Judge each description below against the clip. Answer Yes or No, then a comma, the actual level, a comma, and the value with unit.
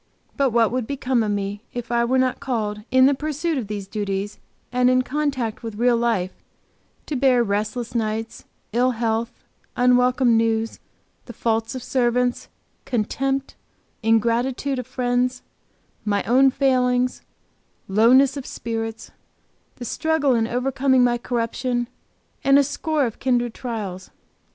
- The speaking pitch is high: Yes, high, 245 Hz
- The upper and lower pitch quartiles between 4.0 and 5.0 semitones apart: No, narrow, 2.4 semitones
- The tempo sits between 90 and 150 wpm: Yes, average, 140 wpm